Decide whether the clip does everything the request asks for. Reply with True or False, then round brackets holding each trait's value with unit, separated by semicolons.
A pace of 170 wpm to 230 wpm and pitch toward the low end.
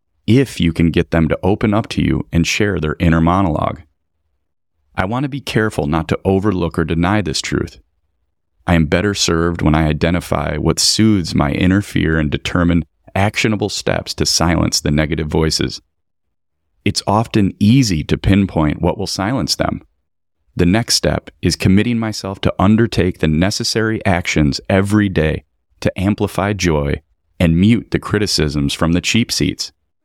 False (160 wpm; 85 Hz)